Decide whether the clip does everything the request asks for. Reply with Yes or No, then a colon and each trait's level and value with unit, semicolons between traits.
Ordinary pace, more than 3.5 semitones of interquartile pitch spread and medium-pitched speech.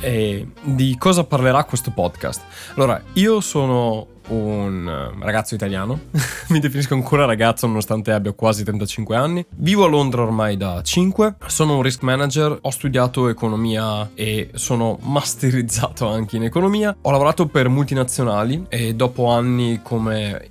No: average, 140 wpm; average, 4.5 semitones; low, 125 Hz